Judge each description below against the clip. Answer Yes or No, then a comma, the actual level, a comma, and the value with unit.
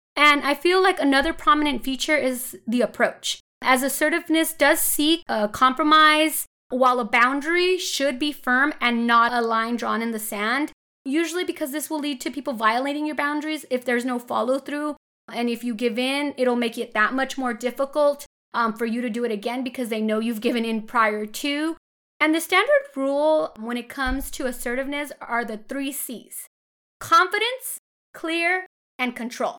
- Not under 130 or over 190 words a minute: Yes, average, 180 wpm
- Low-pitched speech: No, very high, 270 Hz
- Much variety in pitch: No, average, 4.0 semitones